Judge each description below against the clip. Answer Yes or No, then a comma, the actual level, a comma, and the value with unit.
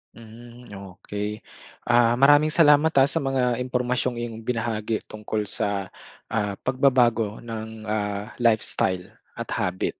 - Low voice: Yes, low, 115 Hz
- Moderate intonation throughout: Yes, average, 3.0 semitones